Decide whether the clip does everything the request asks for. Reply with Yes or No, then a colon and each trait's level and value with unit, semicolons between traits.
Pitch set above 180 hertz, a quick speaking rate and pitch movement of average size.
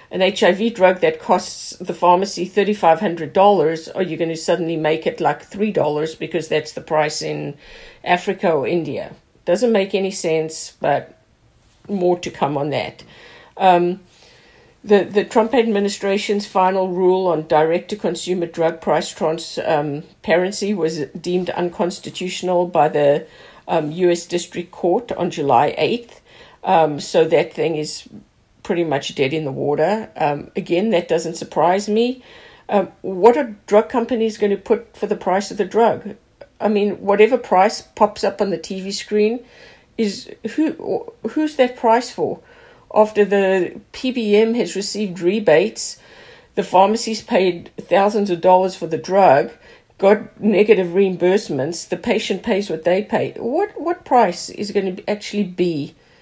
No: high, 190 Hz; average, 155 wpm; average, 3.9 semitones